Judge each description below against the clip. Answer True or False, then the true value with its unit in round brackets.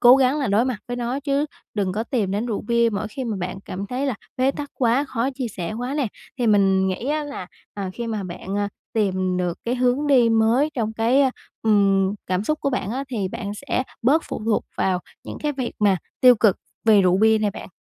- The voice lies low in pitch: False (225 Hz)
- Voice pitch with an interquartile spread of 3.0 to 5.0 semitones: True (4.4 semitones)